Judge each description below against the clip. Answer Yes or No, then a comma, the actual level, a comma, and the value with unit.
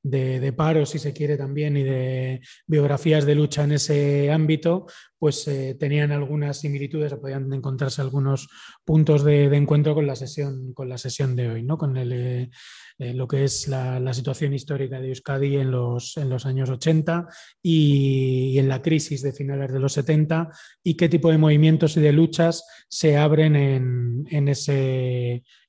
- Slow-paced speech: No, average, 180 wpm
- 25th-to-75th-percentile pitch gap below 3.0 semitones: Yes, narrow, 2.5 semitones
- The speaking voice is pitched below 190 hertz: Yes, medium, 140 Hz